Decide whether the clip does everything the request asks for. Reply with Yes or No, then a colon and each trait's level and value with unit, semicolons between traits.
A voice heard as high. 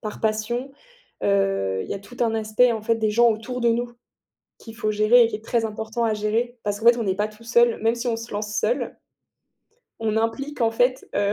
Yes: high, 225 Hz